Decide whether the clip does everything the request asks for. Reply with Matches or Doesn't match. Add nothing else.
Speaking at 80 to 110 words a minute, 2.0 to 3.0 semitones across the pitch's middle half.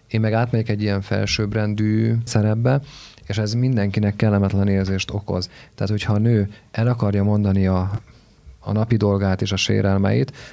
Doesn't match